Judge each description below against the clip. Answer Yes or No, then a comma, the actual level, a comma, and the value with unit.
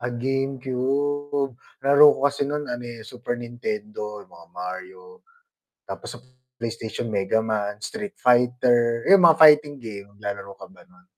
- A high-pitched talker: No, low, 125 Hz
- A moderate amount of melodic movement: Yes, average, 4.6 semitones